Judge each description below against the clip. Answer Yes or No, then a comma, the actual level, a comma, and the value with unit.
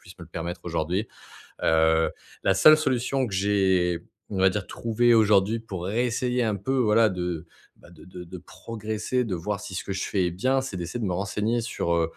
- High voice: No, low, 100 Hz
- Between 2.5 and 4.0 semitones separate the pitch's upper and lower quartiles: No, average, 4.6 semitones